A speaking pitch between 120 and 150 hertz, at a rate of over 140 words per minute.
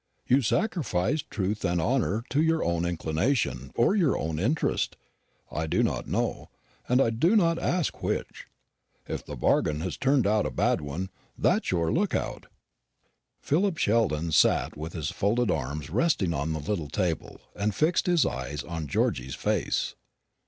No: low, 100 Hz; average, 160 wpm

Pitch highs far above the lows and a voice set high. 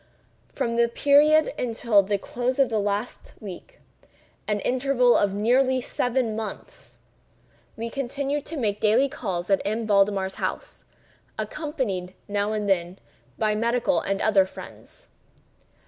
No: average, 4.3 semitones; high, 225 Hz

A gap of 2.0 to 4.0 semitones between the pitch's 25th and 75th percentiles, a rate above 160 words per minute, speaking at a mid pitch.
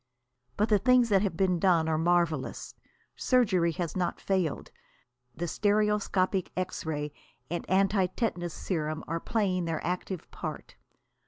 No: average, 3.2 semitones; slow, 135 wpm; medium, 180 Hz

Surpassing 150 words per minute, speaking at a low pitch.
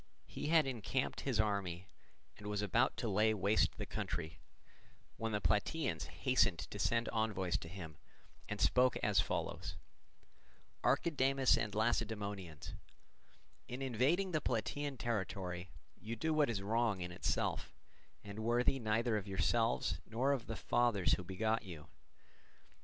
No: average, 140 wpm; low, 110 Hz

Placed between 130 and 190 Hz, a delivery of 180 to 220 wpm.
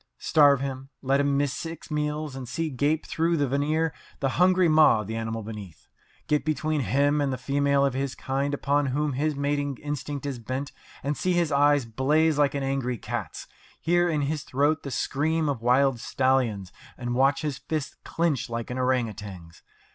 Yes: medium, 140 Hz; average, 190 wpm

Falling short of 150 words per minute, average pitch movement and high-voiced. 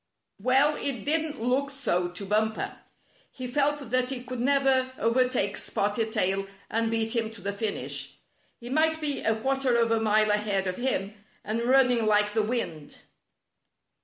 No: average, 160 wpm; average, 4.0 semitones; high, 230 Hz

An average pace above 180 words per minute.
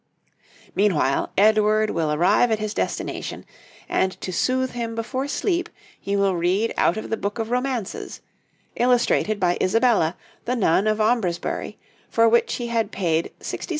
No: average, 155 wpm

